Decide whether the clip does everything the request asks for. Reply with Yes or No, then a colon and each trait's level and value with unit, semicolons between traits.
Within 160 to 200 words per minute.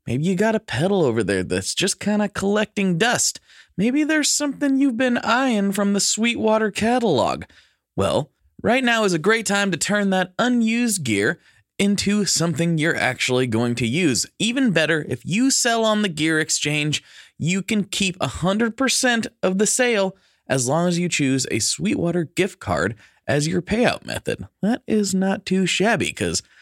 Yes: average, 175 wpm